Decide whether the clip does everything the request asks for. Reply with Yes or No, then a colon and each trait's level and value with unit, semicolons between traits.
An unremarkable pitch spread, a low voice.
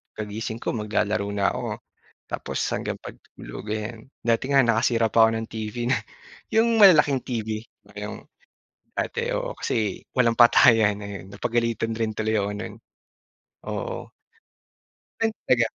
No: narrow, 2.0 semitones; low, 115 Hz